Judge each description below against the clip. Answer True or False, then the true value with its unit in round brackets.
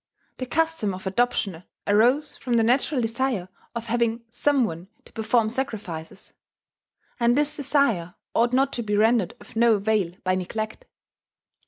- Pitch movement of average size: True (3.8 semitones)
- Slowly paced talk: False (150 wpm)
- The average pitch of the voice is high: True (230 Hz)